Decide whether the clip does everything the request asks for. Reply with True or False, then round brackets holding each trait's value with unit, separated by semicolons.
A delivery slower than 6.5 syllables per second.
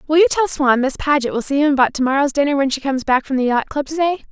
False (6.9 syllables/s)